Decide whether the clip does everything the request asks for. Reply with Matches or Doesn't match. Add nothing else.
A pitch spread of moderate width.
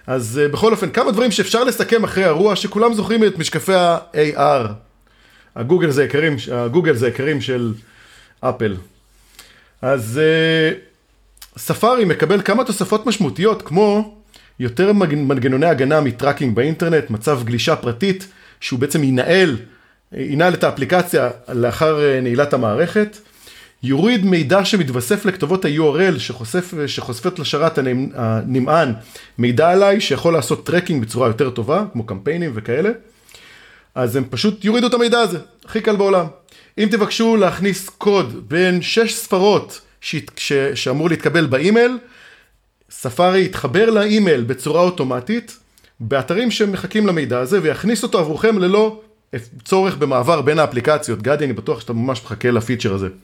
Doesn't match